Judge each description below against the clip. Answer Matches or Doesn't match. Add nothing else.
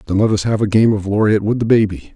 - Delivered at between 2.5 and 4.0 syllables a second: Doesn't match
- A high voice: Doesn't match